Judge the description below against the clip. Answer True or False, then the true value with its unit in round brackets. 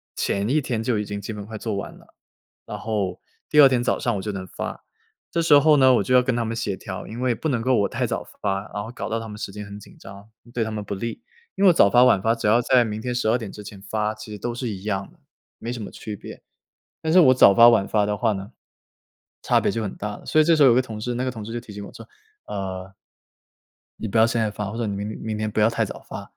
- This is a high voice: False (110 Hz)